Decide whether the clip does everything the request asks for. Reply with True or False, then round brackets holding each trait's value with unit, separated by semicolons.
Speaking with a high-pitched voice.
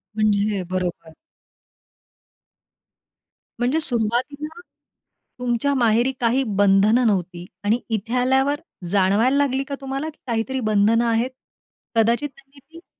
True (235 Hz)